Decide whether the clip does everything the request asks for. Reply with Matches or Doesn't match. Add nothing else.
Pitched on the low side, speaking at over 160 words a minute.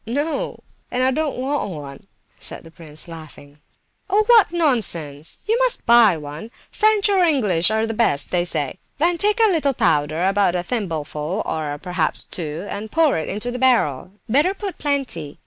Doesn't match